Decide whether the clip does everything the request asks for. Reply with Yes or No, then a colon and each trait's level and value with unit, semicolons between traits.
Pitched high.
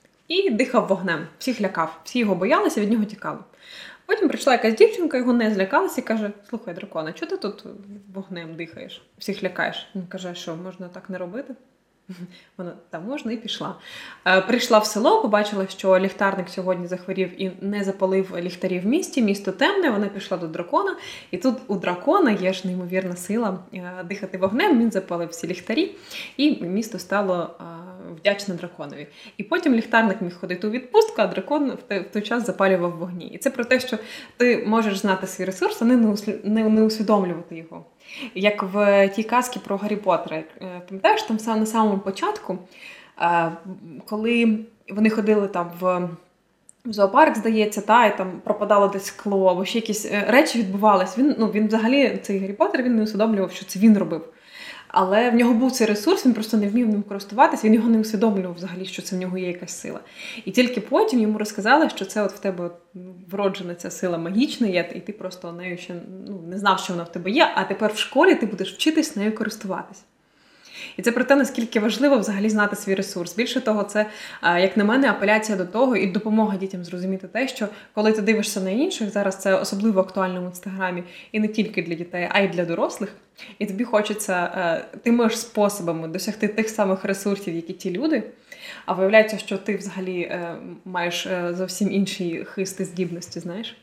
Yes: high, 205 Hz